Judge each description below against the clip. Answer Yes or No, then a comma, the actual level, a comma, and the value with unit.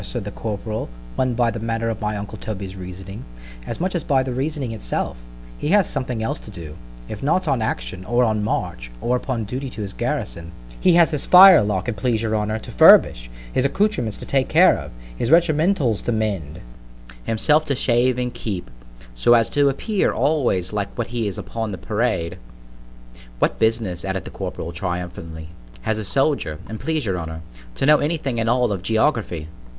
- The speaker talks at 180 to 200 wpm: Yes, average, 185 wpm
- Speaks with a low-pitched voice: Yes, low, 110 Hz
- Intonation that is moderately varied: No, wide, 6.1 semitones